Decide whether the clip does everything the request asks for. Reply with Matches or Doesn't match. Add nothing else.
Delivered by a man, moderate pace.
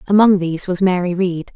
Doesn't match